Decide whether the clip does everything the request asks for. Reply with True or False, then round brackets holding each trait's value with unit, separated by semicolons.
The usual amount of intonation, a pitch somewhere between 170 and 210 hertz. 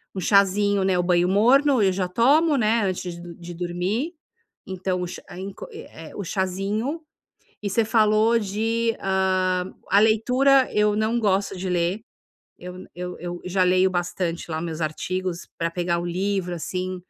True (3.3 semitones; 190 Hz)